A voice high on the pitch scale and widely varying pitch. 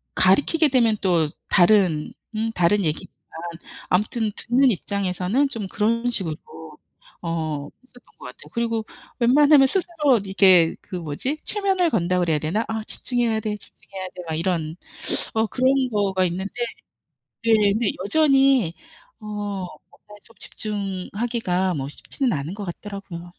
No: high, 205 Hz; average, 4.8 semitones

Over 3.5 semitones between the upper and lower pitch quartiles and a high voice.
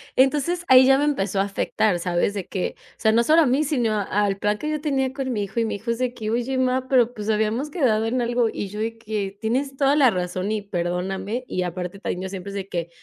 Yes: average, 4.8 semitones; high, 220 Hz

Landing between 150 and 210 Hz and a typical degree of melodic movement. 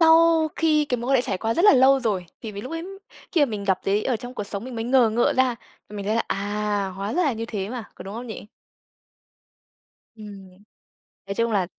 No: high, 230 Hz; average, 4.3 semitones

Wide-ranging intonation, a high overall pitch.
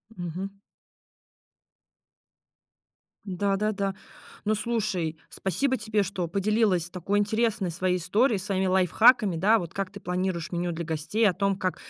No: average, 2.9 semitones; high, 195 Hz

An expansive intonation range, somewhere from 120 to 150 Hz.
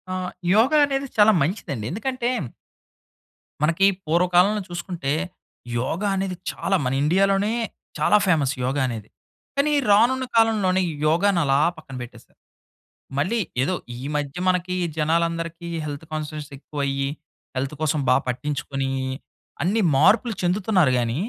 No: wide, 5.7 semitones; medium, 170 Hz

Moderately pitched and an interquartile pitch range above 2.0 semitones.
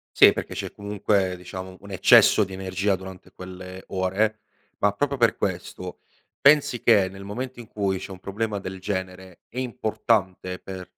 No: very low, 95 Hz; narrow, 2.4 semitones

